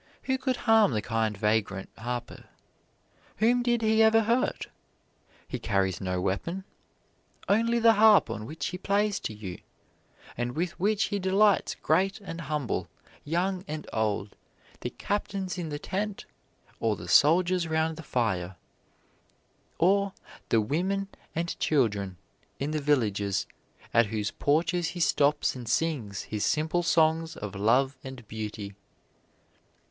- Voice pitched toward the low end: No, medium, 155 Hz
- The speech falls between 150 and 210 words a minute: No, average, 140 wpm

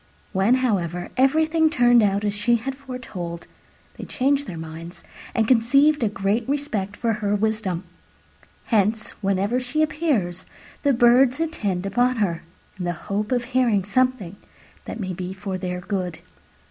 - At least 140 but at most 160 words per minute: Yes, average, 150 wpm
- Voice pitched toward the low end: No, high, 215 Hz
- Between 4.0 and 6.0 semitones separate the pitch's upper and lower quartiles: Yes, average, 5.2 semitones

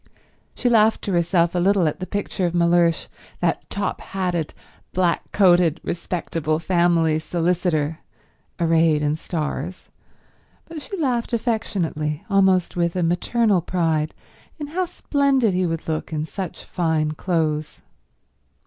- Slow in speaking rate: Yes, slow, 130 wpm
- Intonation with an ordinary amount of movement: Yes, average, 3.2 semitones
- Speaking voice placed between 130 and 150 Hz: No, medium, 175 Hz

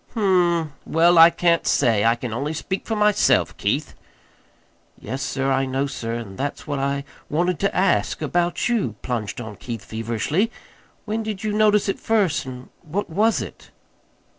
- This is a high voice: No, medium, 155 Hz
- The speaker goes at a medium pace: Yes, average, 170 wpm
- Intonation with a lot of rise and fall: Yes, wide, 7.4 semitones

